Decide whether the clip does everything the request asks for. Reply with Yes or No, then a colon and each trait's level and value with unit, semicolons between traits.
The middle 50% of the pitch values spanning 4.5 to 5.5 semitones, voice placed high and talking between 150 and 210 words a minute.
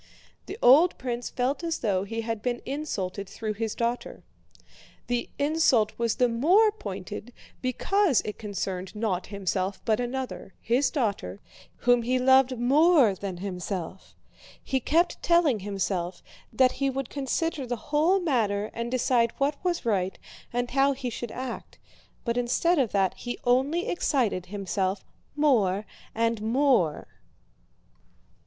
No: average, 5.1 semitones; high, 240 Hz; average, 140 wpm